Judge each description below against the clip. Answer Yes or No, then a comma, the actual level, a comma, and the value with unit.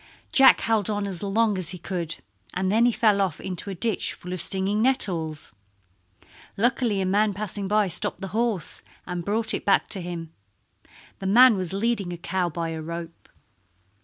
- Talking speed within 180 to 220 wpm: Yes, average, 185 wpm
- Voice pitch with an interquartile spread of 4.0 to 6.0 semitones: No, average, 3.3 semitones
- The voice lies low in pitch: No, high, 195 Hz